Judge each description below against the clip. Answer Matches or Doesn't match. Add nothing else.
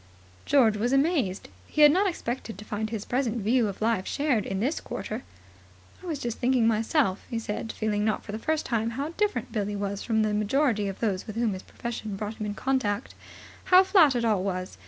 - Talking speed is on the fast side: Matches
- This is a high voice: Matches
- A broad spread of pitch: Doesn't match